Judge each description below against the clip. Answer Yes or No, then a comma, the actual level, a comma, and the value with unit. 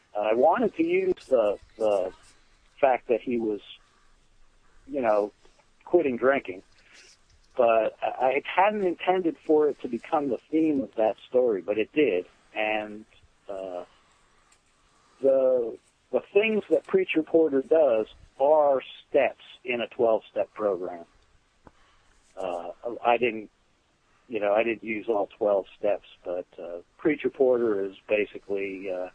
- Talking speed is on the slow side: Yes, slow, 130 wpm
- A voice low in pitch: Yes, low, 125 Hz